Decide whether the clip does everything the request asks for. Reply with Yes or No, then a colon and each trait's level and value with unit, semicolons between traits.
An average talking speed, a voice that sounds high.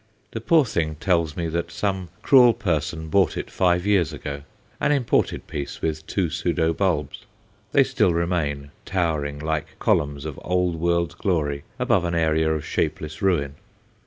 No: average, 160 wpm; very low, 85 Hz